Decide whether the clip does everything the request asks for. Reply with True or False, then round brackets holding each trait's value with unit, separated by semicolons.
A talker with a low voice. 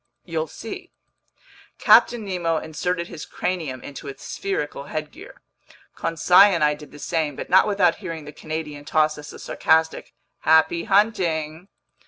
False (160 Hz)